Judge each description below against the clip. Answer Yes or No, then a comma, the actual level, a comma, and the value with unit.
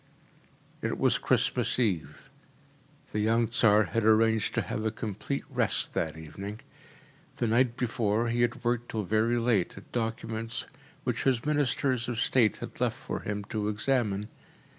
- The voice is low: Yes, low, 115 Hz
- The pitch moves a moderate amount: No, narrow, 2.2 semitones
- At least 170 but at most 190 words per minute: No, average, 155 wpm